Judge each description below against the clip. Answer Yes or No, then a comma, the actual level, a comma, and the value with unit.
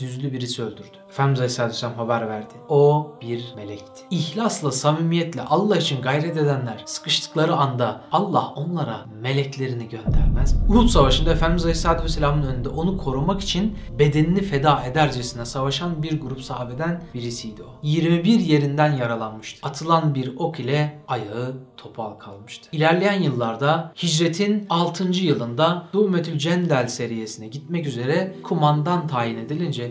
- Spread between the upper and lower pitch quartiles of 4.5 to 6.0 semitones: Yes, average, 5.1 semitones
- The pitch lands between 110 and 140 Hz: No, medium, 150 Hz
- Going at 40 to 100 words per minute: No, average, 130 wpm